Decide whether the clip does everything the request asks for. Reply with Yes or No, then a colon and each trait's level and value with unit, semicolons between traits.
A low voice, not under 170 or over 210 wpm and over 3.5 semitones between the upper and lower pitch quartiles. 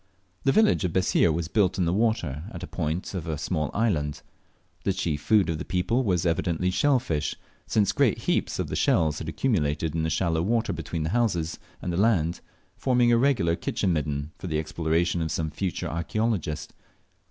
Yes: very low, 85 Hz; average, 195 wpm; average, 4.7 semitones